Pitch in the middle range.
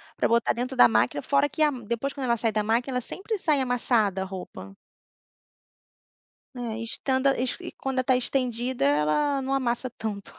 No: high, 245 Hz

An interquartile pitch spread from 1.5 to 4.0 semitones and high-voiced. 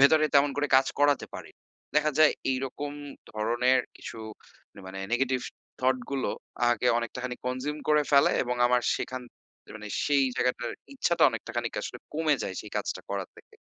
No: average, 2.9 semitones; low, 130 Hz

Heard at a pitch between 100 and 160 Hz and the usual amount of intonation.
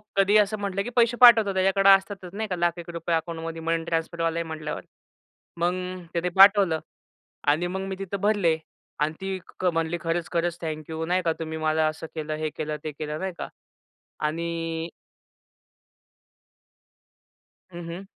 No: medium, 170 Hz; average, 3.0 semitones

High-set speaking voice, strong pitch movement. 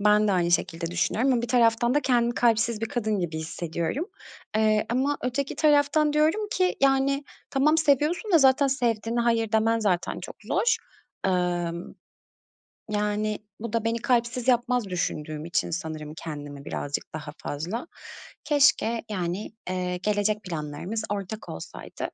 Yes: high, 220 Hz; wide, 6.5 semitones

